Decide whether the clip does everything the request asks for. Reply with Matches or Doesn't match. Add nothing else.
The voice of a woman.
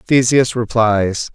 Doesn't match